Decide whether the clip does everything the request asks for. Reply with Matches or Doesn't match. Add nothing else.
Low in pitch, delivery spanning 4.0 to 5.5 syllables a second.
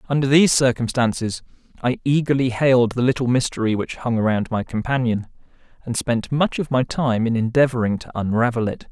Doesn't match